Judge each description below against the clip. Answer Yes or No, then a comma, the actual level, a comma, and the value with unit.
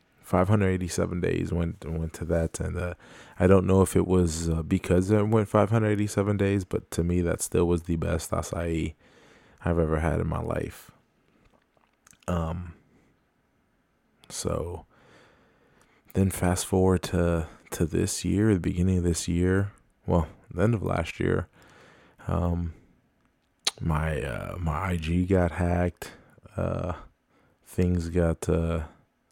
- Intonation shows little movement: Yes, narrow, 2.3 semitones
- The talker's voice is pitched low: Yes, very low, 90 Hz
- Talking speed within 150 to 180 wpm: No, slow, 135 wpm